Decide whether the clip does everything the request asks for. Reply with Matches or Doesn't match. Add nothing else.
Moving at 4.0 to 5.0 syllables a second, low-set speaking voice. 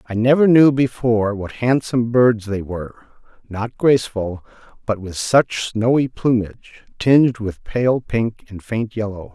Matches